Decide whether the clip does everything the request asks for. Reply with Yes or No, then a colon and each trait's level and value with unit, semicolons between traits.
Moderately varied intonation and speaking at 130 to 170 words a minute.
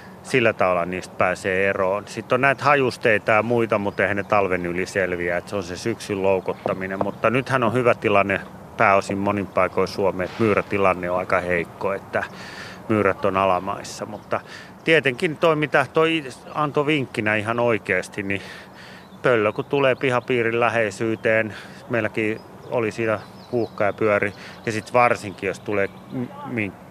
Yes: average, 4.0 semitones; average, 150 wpm